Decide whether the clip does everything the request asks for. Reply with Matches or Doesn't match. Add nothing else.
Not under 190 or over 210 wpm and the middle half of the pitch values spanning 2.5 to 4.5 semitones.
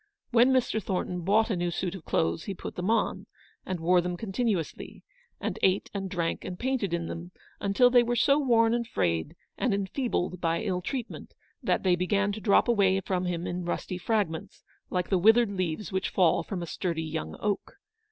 Matches